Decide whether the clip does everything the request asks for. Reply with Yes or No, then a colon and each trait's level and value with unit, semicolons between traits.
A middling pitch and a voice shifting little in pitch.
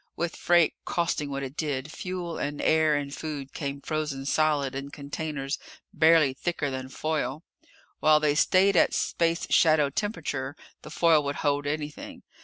Yes: medium, 150 Hz; narrow, 2.3 semitones